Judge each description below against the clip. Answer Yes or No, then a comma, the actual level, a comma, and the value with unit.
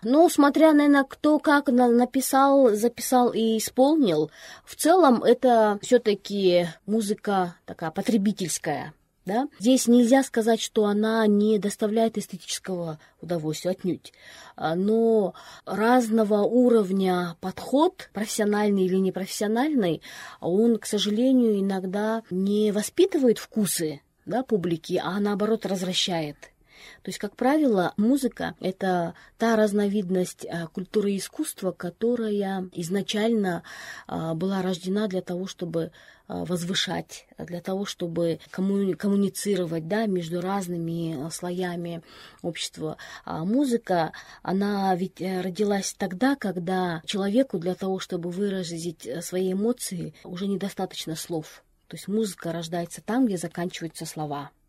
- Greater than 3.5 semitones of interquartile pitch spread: Yes, average, 4.0 semitones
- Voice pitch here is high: Yes, high, 200 Hz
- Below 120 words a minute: Yes, slow, 110 wpm